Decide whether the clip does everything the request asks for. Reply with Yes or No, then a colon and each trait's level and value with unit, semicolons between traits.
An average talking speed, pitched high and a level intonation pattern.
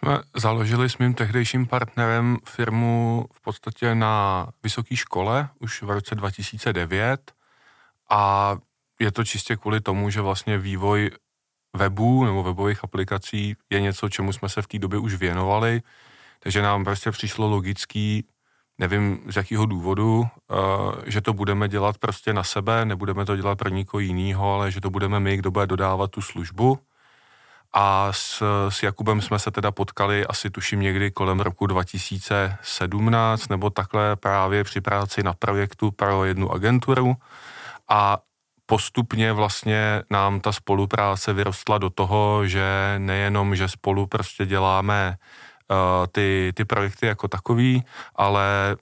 No: average, 145 wpm; low, 100 Hz; narrow, 2.1 semitones